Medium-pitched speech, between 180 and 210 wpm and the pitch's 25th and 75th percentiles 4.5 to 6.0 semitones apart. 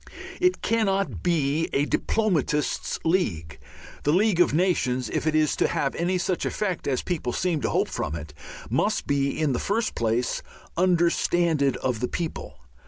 No: medium, 160 Hz; average, 165 wpm; average, 5.0 semitones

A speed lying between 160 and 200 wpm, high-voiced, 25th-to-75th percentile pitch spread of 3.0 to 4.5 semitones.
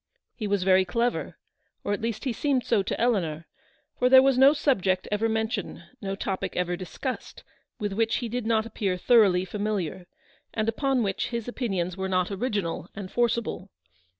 Yes: average, 175 wpm; high, 210 Hz; average, 4.1 semitones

